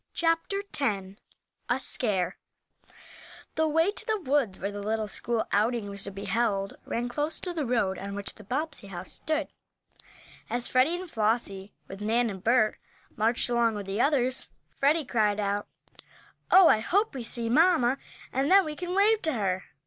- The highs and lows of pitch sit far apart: Yes, wide, 7.0 semitones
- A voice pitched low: No, high, 235 Hz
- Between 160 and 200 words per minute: Yes, average, 175 wpm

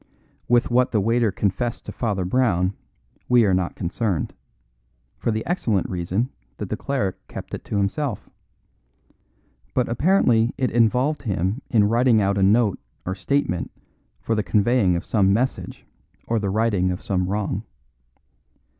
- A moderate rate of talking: Yes, average, 150 wpm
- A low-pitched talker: Yes, low, 110 Hz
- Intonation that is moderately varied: Yes, average, 4.1 semitones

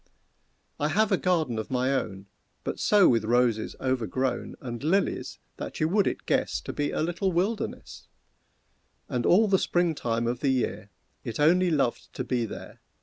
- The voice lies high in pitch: No, low, 135 Hz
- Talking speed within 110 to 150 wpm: No, average, 175 wpm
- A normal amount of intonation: No, wide, 6.7 semitones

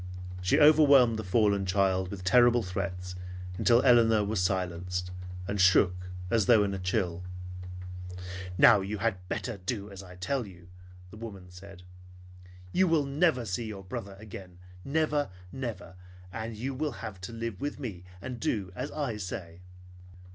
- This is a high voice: No, low, 100 Hz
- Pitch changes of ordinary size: Yes, average, 4.6 semitones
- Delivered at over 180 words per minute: No, average, 155 wpm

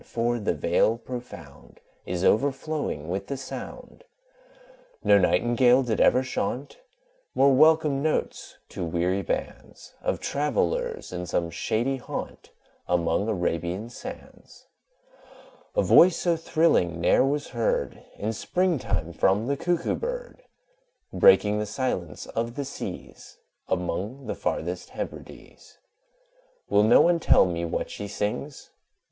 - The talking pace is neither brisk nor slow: No, slow, 125 wpm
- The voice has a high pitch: No, low, 120 Hz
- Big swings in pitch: Yes, wide, 7.7 semitones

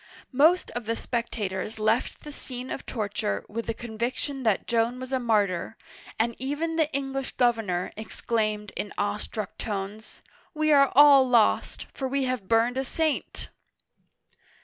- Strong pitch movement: No, average, 3.9 semitones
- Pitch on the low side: No, high, 235 Hz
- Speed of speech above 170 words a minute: No, average, 150 wpm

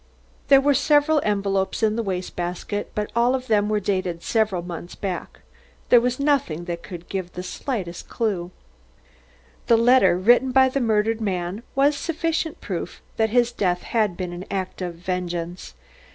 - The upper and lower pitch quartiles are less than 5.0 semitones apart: No, average, 5.3 semitones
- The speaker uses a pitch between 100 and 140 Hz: No, high, 205 Hz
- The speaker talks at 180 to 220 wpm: No, average, 165 wpm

